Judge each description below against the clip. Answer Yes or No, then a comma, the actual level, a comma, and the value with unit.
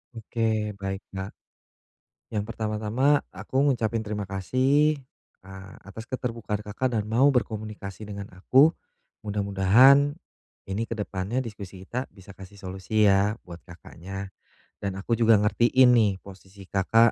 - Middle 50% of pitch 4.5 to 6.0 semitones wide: No, average, 3.2 semitones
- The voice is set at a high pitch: No, low, 105 Hz